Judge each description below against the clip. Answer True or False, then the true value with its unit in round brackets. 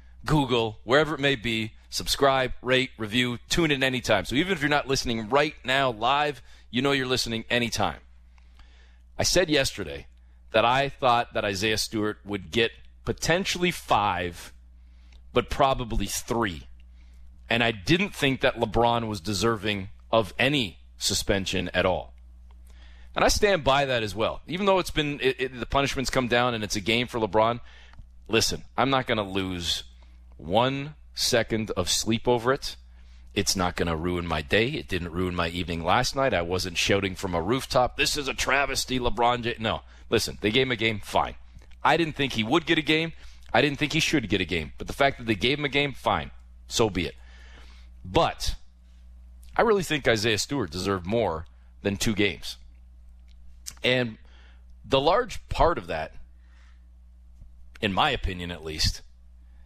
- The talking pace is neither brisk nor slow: True (175 wpm)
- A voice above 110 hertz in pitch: False (105 Hz)